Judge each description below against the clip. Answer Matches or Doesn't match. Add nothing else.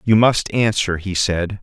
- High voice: Doesn't match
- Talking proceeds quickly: Doesn't match